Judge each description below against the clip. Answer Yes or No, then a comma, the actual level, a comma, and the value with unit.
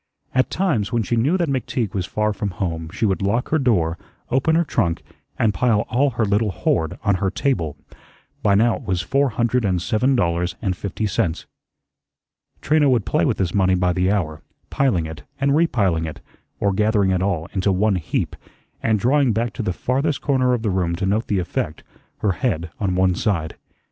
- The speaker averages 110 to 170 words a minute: No, average, 200 wpm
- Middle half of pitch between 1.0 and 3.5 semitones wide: No, average, 5.2 semitones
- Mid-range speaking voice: No, low, 105 Hz